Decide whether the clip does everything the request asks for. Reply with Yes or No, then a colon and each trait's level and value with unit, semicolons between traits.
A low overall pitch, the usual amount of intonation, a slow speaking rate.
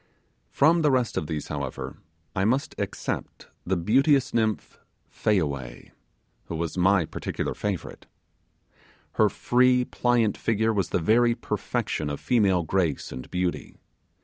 No: low, 100 Hz; wide, 6.5 semitones; slow, 130 wpm